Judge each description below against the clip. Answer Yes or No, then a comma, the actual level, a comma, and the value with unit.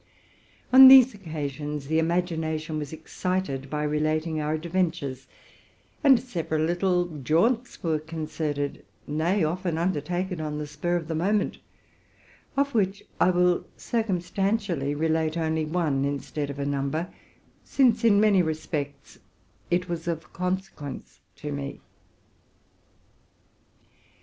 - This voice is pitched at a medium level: Yes, medium, 160 Hz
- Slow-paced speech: Yes, slow, 125 wpm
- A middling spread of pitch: Yes, average, 3.4 semitones